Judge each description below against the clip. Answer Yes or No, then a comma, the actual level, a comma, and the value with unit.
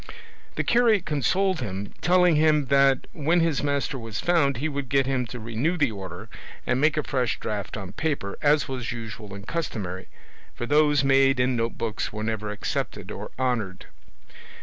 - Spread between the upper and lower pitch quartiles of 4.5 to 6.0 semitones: Yes, average, 5.3 semitones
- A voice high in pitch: No, low, 135 Hz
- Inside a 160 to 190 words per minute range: Yes, average, 170 wpm